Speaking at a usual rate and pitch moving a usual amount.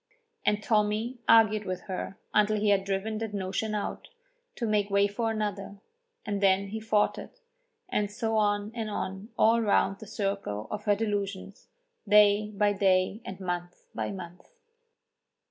No: average, 160 wpm; narrow, 1.6 semitones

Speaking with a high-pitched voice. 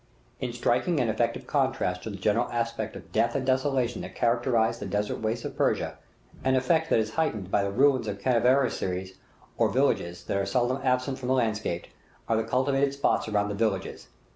No: low, 115 Hz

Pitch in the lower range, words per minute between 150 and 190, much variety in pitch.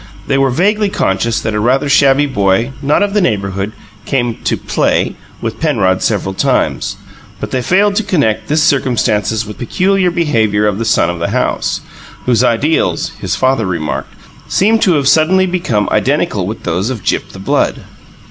Yes: low, 125 Hz; average, 175 wpm; wide, 7.4 semitones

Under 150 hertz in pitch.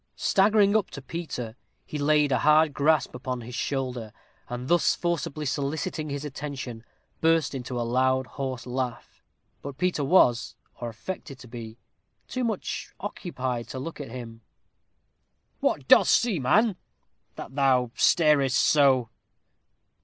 Yes: low, 135 Hz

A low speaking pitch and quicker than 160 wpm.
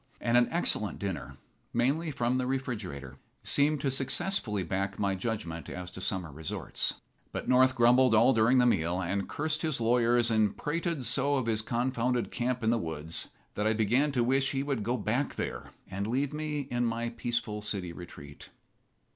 Yes: low, 120 Hz; average, 180 wpm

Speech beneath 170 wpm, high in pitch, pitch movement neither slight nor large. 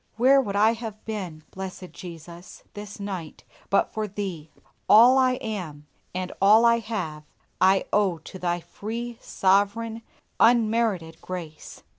Yes: slow, 135 wpm; high, 200 Hz; average, 4.0 semitones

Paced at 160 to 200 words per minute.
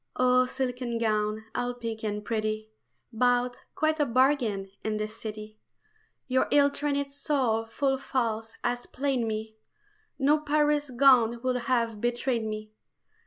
No: slow, 135 wpm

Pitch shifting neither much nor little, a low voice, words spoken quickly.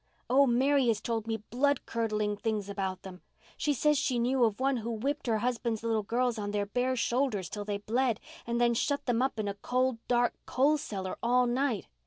No: average, 3.3 semitones; high, 235 Hz; fast, 210 wpm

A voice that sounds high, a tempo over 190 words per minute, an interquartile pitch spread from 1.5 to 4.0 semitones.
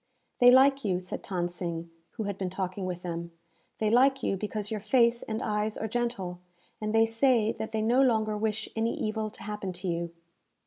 Yes: high, 215 Hz; fast, 205 wpm; average, 3.5 semitones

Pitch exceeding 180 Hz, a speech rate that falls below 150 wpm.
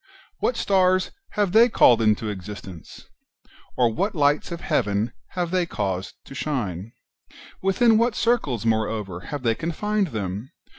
No: low, 130 Hz; average, 140 wpm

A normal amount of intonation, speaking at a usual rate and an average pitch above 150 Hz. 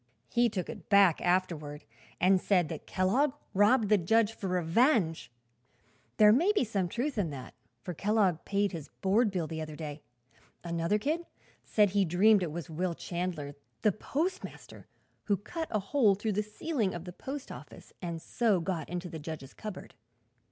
Yes: average, 4.4 semitones; average, 175 wpm; high, 190 Hz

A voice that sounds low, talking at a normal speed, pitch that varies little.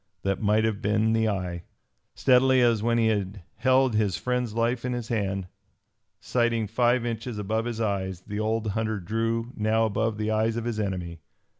Yes: low, 110 Hz; average, 180 wpm; narrow, 2.2 semitones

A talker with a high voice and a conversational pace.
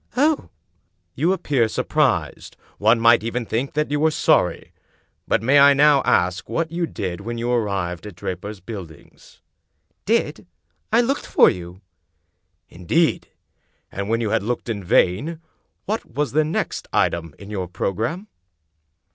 No: low, 115 Hz; average, 150 wpm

